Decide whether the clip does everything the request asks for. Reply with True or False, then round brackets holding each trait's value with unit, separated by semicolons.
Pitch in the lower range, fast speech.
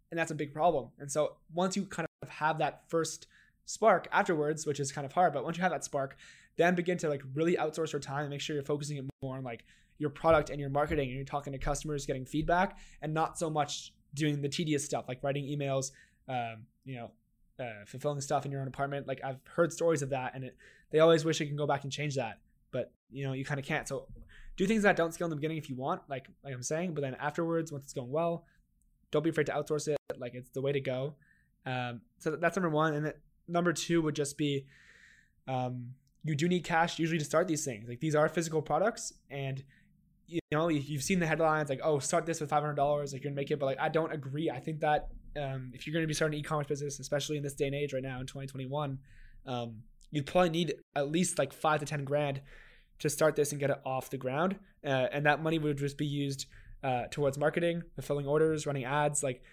False (145 Hz; 250 wpm)